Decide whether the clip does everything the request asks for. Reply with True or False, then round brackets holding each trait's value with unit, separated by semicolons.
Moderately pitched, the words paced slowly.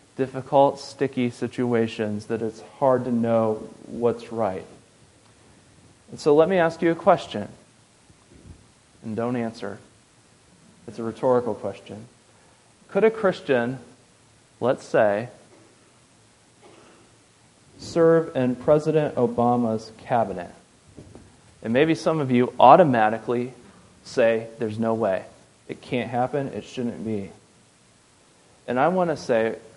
False (120 Hz; 115 wpm)